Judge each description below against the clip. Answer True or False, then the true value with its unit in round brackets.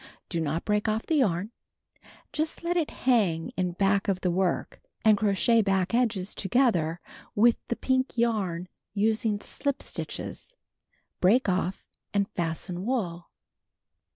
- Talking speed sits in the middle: True (155 wpm)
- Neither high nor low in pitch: False (205 Hz)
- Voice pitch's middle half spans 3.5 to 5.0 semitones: True (4.6 semitones)